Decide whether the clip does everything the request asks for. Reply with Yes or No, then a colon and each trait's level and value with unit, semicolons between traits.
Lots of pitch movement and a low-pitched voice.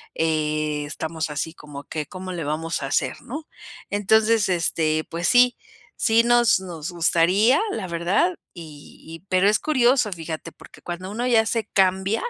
No: wide, 5.7 semitones; medium, 180 Hz